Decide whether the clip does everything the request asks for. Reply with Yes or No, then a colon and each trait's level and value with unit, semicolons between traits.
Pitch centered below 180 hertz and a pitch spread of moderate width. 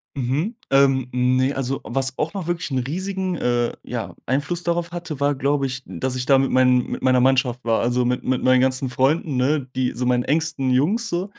Yes: low, 135 Hz; average, 3.5 semitones